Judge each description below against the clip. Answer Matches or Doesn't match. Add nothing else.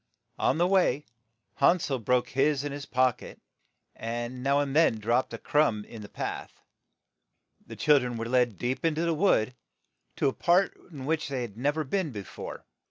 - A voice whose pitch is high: Doesn't match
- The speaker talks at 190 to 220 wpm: Matches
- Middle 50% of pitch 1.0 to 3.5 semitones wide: Doesn't match